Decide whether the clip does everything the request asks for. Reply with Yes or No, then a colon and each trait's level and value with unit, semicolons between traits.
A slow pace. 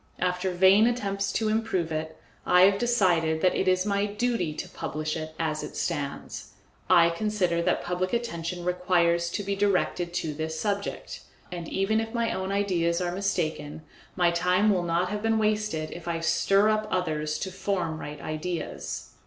No: average, 175 wpm